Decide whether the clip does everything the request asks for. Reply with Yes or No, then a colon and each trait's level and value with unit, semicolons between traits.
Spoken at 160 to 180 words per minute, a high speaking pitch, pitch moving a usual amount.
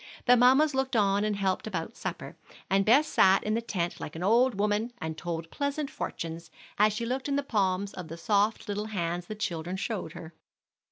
No: fast, 205 wpm; high, 205 Hz; average, 4.8 semitones